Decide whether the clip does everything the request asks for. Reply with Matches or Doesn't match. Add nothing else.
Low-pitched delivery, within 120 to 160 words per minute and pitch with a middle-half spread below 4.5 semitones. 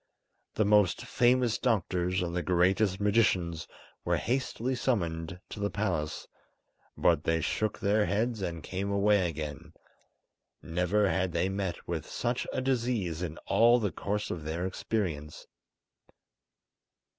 Matches